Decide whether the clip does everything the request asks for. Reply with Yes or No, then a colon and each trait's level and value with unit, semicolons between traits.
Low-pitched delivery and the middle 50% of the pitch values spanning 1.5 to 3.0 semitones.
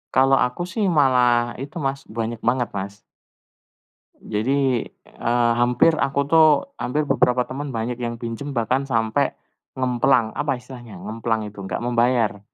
Yes: low, 125 Hz; average, 2.7 semitones